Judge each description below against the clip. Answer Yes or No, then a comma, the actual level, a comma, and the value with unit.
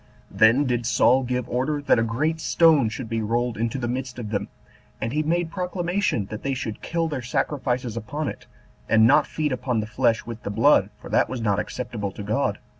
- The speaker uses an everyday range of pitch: Yes, average, 4.5 semitones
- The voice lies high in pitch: No, low, 125 Hz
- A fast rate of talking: Yes, fast, 210 wpm